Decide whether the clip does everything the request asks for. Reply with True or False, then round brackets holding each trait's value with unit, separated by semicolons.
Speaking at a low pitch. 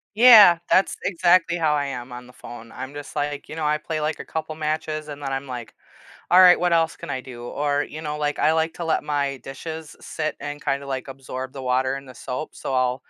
False (145 Hz)